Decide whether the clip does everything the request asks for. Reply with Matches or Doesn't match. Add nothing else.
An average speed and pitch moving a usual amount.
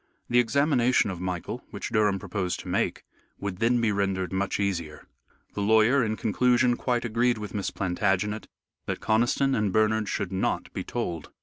Matches